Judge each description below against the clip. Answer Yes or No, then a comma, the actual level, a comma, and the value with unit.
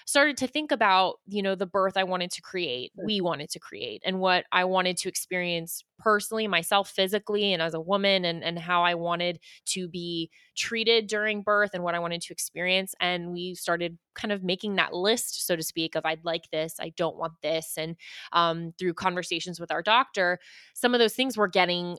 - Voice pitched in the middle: Yes, medium, 180 Hz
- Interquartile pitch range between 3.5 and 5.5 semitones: No, average, 2.9 semitones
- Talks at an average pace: No, fast, 210 wpm